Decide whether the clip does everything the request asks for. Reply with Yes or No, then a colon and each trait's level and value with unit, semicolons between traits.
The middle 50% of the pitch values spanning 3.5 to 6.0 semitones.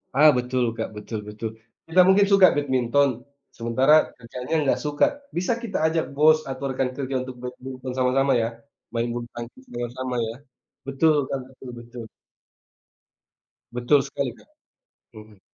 No: average, 3.1 semitones